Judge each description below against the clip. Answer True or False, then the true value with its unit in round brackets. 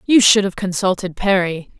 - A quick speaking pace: False (165 wpm)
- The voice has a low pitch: False (190 Hz)